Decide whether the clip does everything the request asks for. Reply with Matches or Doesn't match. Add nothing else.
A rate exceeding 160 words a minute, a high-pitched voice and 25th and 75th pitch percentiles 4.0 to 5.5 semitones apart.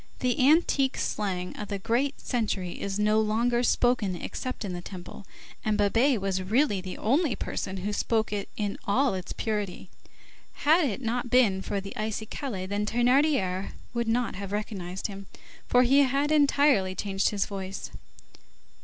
Doesn't match